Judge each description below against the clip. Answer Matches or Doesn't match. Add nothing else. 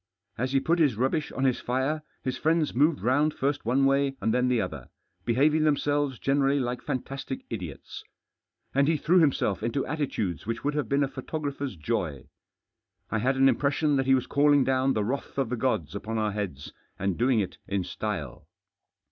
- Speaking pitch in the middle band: Doesn't match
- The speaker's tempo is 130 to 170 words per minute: Doesn't match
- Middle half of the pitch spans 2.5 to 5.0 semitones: Matches